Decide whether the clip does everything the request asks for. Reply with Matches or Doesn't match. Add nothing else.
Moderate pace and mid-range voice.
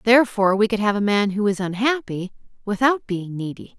Doesn't match